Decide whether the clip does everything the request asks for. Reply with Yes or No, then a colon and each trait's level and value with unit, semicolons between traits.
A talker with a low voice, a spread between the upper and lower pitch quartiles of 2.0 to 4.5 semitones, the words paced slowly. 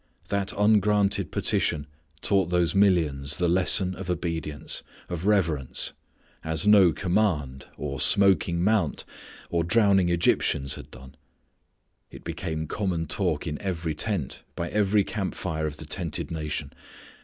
Yes: very low, 85 Hz; average, 4.2 semitones; slow, 130 wpm